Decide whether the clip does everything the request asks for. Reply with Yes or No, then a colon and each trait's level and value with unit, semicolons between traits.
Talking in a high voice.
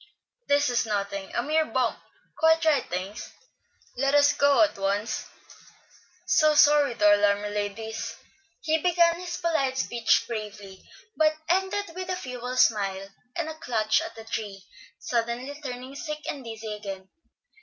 Yes: high, 245 Hz